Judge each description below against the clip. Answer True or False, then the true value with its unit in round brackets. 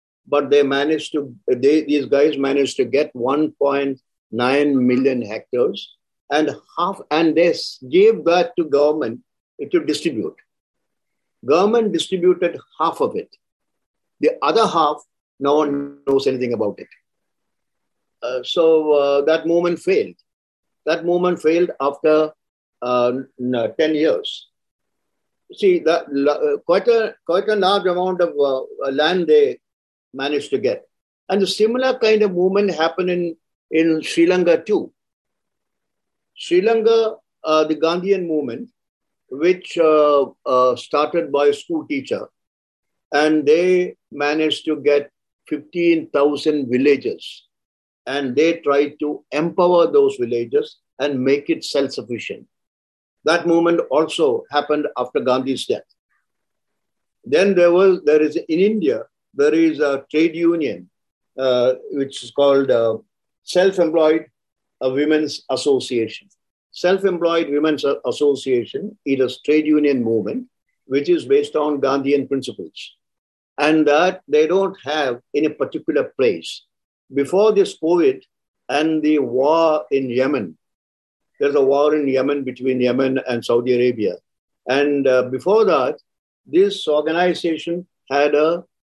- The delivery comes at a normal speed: False (130 wpm)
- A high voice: False (155 Hz)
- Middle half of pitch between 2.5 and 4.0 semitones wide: False (5.1 semitones)